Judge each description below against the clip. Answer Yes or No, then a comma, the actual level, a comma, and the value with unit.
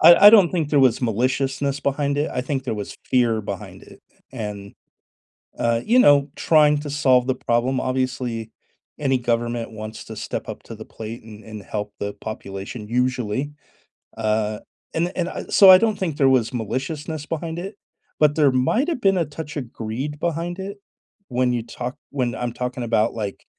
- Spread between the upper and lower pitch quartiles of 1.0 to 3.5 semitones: No, average, 4.7 semitones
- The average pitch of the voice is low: Yes, low, 130 Hz